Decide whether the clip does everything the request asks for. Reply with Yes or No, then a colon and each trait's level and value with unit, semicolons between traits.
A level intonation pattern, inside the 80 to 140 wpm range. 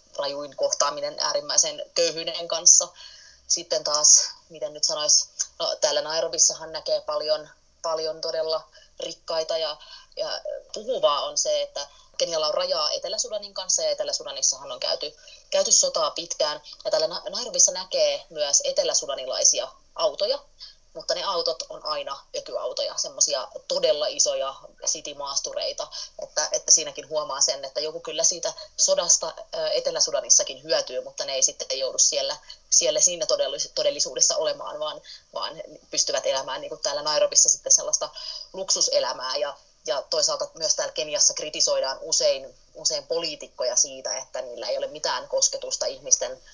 Yes: narrow, 2.1 semitones; average, 135 wpm